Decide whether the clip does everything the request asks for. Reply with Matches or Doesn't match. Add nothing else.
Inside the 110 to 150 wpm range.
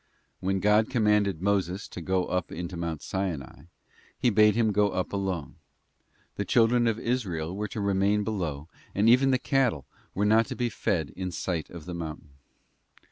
Doesn't match